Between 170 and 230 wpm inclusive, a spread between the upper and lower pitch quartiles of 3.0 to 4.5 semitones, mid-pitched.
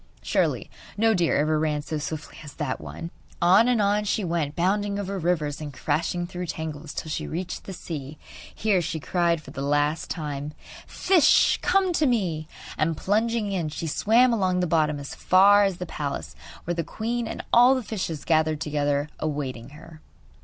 No: average, 180 wpm; average, 5.0 semitones; medium, 170 Hz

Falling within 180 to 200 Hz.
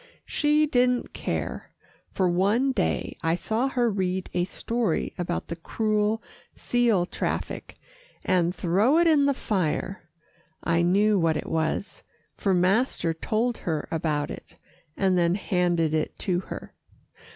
Yes: high, 190 Hz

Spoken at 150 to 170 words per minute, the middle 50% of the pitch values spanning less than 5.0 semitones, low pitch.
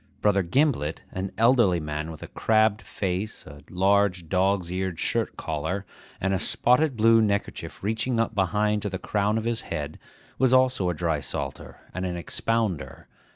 Yes: average, 160 wpm; average, 4.3 semitones; low, 100 Hz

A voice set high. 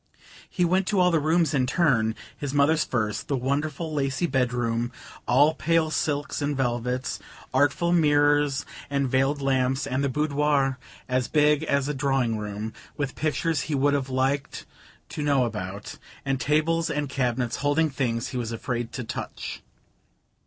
No: medium, 140 Hz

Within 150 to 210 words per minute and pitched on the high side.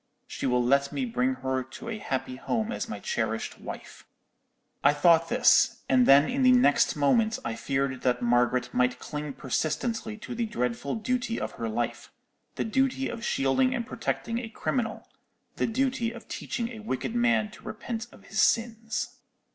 Yes: average, 170 wpm; high, 215 Hz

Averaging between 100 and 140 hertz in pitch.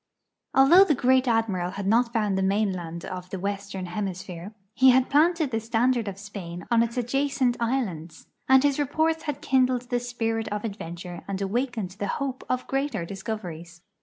No: high, 225 Hz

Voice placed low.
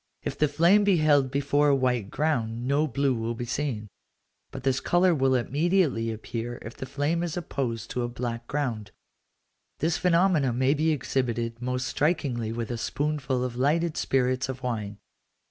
Yes: low, 130 Hz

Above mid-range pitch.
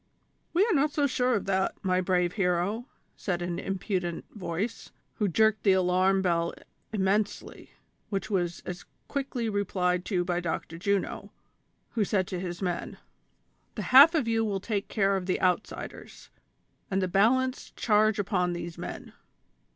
Yes: high, 195 Hz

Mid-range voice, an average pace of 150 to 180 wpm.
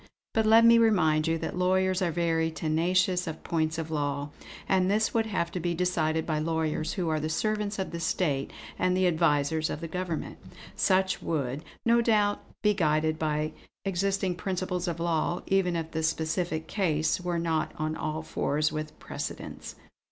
Yes: medium, 170 Hz; average, 175 wpm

